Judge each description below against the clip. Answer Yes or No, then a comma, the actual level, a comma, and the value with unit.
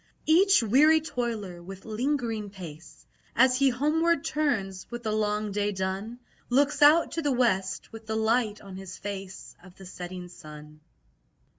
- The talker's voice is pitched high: Yes, high, 215 Hz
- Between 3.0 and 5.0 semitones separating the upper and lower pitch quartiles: No, wide, 5.4 semitones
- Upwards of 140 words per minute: Yes, average, 155 wpm